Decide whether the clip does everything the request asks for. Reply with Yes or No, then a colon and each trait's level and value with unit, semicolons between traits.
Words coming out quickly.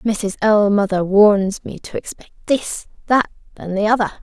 No: average, 155 wpm